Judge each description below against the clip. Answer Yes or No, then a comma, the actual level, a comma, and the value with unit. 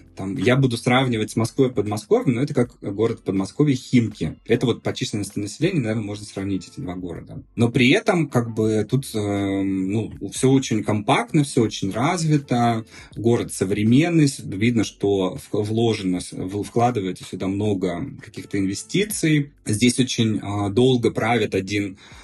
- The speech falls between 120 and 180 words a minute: Yes, average, 145 wpm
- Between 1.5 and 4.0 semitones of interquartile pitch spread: No, average, 4.4 semitones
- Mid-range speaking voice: No, low, 110 Hz